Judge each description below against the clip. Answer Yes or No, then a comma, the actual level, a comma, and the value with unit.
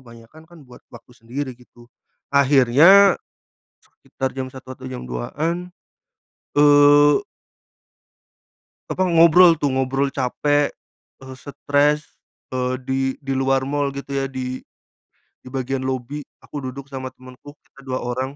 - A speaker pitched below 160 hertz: Yes, low, 135 Hz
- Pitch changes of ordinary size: No, narrow, 2.1 semitones